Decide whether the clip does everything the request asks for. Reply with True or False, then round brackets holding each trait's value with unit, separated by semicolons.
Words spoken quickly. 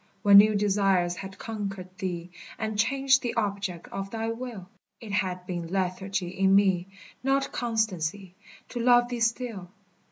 False (150 wpm)